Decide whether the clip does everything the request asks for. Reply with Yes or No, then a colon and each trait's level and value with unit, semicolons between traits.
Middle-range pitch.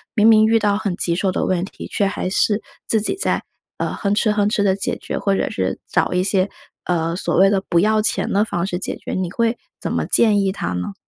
No: high, 200 Hz